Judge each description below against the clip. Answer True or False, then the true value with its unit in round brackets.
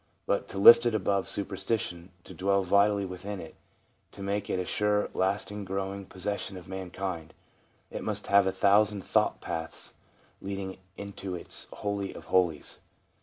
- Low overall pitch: True (100 Hz)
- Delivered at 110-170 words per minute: True (155 wpm)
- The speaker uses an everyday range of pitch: False (1.5 semitones)